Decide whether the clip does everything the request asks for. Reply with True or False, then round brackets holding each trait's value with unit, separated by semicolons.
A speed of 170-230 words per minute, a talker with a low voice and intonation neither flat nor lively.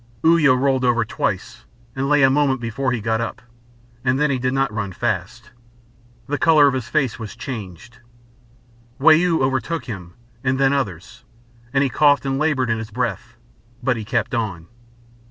True (175 wpm; 130 Hz; 3.6 semitones)